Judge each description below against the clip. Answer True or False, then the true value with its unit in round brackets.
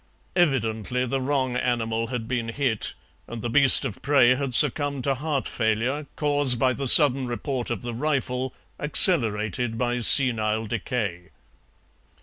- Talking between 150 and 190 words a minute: False (140 wpm)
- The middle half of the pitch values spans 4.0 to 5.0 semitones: False (3.3 semitones)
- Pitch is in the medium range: False (125 Hz)